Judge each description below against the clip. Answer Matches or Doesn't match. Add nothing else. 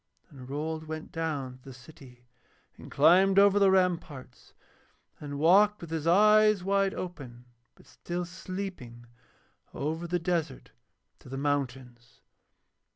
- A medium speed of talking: Doesn't match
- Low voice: Doesn't match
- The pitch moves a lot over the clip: Matches